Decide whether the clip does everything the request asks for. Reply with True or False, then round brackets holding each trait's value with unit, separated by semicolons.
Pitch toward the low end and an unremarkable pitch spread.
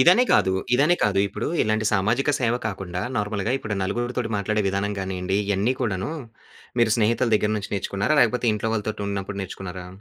True (105 Hz; 3.0 semitones)